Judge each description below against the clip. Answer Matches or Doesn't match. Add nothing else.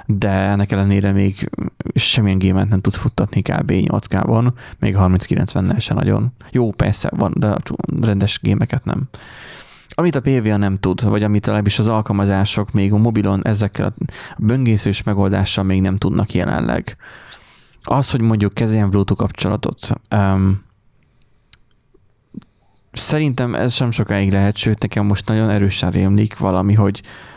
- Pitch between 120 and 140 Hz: Doesn't match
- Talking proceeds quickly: Doesn't match